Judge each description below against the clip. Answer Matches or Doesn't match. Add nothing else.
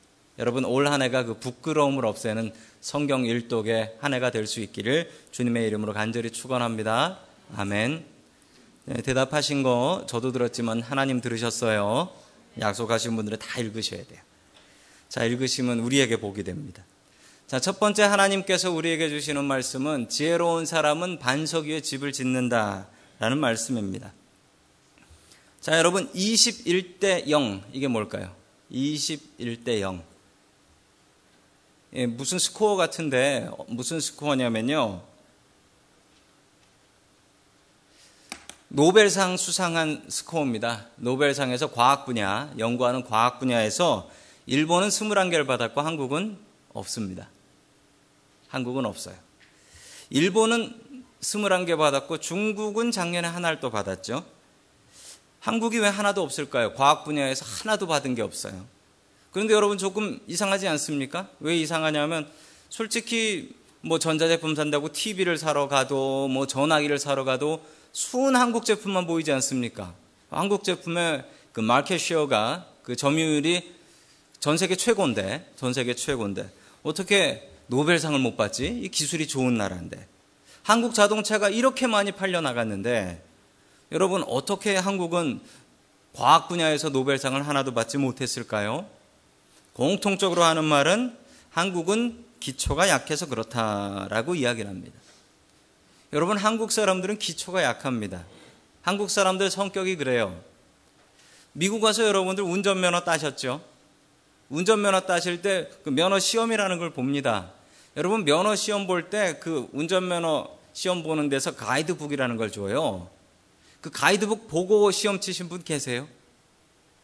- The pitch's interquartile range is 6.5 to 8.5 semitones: Matches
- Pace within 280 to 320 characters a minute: Matches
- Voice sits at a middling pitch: Matches